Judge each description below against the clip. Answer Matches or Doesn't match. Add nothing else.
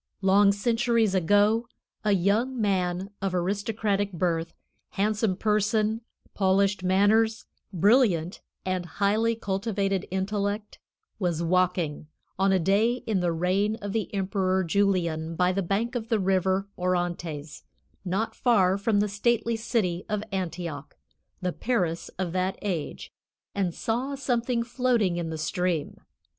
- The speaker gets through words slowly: Matches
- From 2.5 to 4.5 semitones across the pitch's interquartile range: Matches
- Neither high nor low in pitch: Doesn't match